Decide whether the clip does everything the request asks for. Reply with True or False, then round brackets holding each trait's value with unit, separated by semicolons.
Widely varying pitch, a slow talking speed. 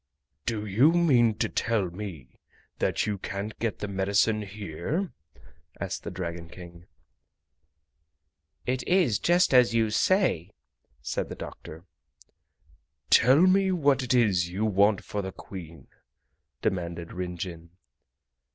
True (6.0 semitones; 125 wpm)